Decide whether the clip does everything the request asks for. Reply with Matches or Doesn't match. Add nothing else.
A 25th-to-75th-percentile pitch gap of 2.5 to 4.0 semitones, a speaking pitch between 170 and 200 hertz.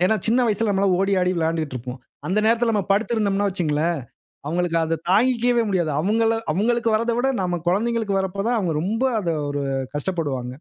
Doesn't match